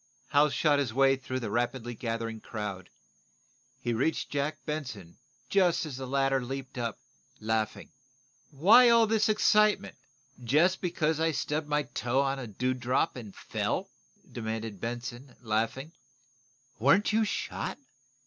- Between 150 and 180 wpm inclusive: No, average, 140 wpm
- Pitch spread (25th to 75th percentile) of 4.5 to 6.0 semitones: Yes, average, 4.9 semitones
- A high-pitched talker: No, low, 135 Hz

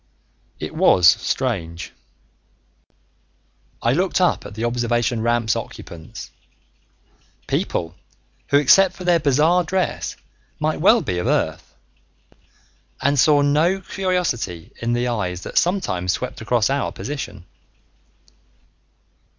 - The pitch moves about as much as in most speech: No, wide, 7.7 semitones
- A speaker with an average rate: No, slow, 110 wpm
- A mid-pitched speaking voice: No, low, 125 Hz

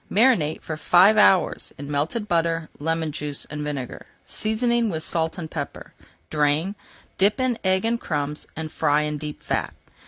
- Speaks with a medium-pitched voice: Yes, medium, 160 Hz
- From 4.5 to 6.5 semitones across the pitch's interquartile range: Yes, average, 5.1 semitones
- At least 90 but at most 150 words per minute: No, average, 160 wpm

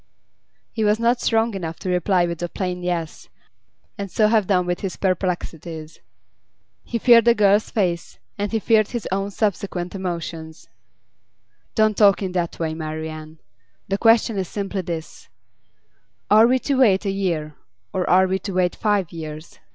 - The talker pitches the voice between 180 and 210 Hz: Yes, high, 190 Hz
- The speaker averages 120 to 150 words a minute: No, average, 165 wpm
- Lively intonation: No, average, 3.7 semitones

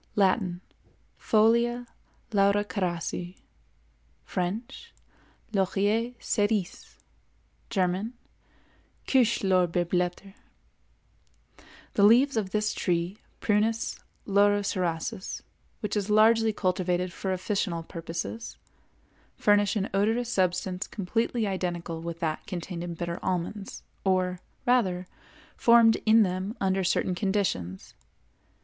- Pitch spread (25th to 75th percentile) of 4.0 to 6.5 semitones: No, average, 3.2 semitones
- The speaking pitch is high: Yes, high, 195 Hz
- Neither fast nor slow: No, slow, 80 wpm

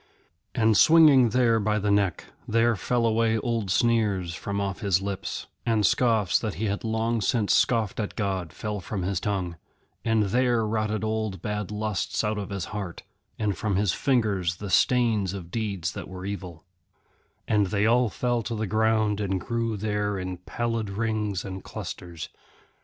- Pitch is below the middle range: Yes, low, 105 Hz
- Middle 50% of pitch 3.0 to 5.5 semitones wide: No, narrow, 2.6 semitones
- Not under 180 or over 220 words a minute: No, average, 170 wpm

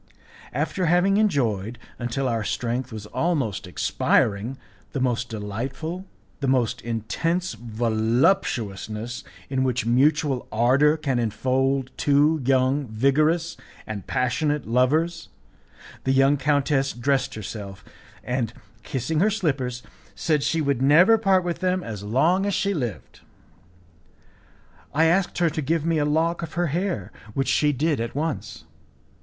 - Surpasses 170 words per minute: No, slow, 135 wpm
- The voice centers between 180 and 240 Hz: No, low, 135 Hz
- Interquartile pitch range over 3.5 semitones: Yes, average, 5.2 semitones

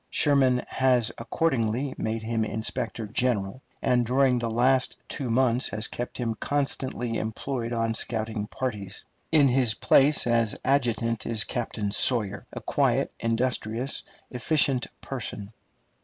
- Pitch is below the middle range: Yes, low, 120 Hz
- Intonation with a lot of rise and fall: No, narrow, 2.6 semitones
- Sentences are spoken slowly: Yes, slow, 125 wpm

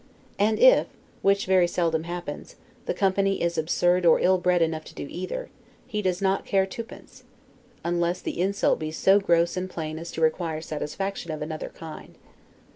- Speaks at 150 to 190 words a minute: Yes, average, 175 wpm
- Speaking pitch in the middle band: Yes, medium, 175 Hz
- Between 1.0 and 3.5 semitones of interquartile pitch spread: Yes, average, 2.9 semitones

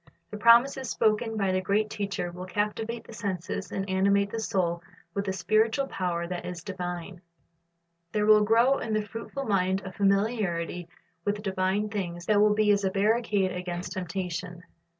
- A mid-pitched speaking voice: No, high, 200 Hz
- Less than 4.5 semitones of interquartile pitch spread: Yes, average, 2.8 semitones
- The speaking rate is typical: Yes, average, 170 wpm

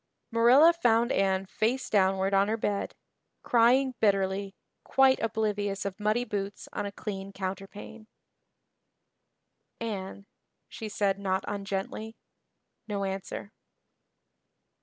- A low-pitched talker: No, high, 205 Hz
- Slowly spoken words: Yes, slow, 105 wpm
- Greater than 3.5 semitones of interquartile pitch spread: No, narrow, 2.6 semitones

